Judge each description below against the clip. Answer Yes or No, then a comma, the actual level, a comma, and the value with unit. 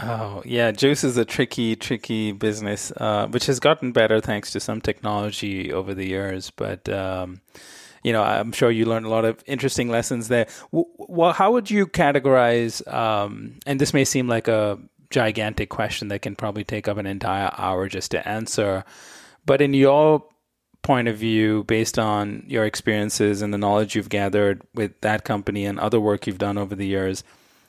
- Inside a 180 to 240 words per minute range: Yes, average, 185 wpm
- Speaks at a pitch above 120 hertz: No, low, 110 Hz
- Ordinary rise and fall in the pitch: Yes, average, 3.5 semitones